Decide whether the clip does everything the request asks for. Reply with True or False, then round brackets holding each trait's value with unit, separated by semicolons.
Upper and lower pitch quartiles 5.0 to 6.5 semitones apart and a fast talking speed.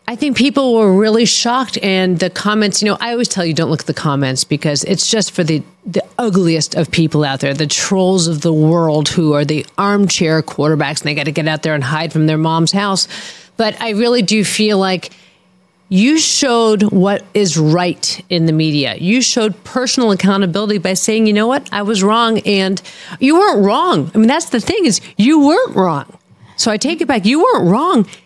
True (5.5 semitones; 215 wpm)